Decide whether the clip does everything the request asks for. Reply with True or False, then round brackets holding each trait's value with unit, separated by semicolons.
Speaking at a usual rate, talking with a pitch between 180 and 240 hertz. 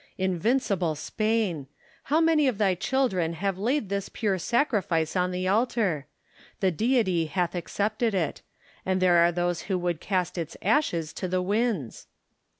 True (150 wpm; 190 Hz)